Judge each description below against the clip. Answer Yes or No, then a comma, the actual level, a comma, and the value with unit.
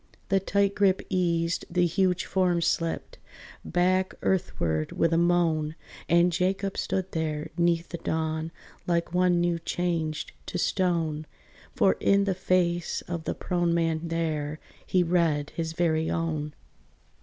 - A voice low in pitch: No, medium, 170 Hz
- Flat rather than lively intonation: Yes, narrow, 2.0 semitones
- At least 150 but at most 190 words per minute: No, average, 140 wpm